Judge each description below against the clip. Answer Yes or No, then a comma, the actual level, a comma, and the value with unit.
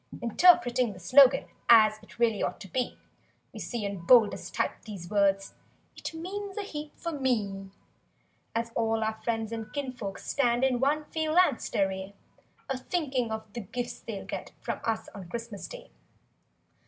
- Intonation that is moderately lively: Yes, average, 4.4 semitones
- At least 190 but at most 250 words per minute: No, average, 165 wpm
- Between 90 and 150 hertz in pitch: No, high, 235 Hz